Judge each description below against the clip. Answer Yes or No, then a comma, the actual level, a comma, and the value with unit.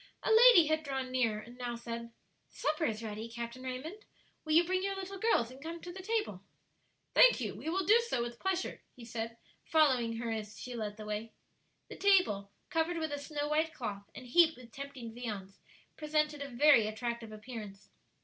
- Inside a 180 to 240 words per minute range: Yes, average, 195 wpm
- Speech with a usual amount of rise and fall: No, wide, 5.9 semitones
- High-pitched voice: Yes, very high, 255 Hz